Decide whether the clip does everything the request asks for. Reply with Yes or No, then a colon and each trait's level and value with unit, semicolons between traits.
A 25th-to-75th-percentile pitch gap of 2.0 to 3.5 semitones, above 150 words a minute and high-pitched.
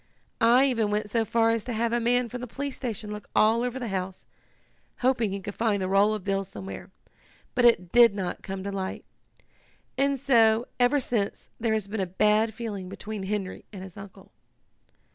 Yes: average, 3.2 semitones; average, 200 wpm; high, 215 Hz